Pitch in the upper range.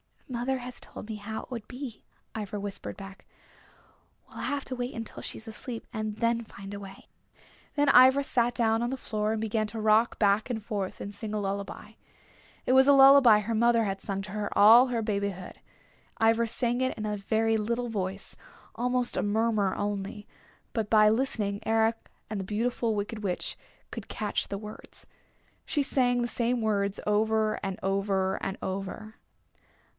Yes: high, 220 Hz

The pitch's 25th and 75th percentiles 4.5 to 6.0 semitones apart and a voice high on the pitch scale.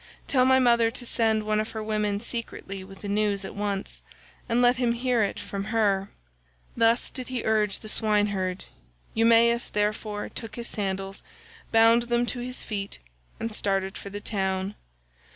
No: average, 2.7 semitones; high, 215 Hz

